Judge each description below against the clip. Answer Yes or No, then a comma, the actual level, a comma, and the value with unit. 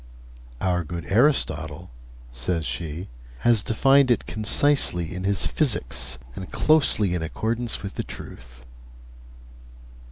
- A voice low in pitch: Yes, very low, 95 Hz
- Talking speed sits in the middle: No, slow, 115 wpm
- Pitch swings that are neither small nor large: No, wide, 6.5 semitones